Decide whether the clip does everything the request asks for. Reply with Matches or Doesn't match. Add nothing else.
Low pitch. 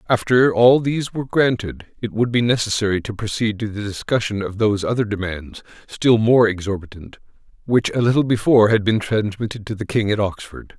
Matches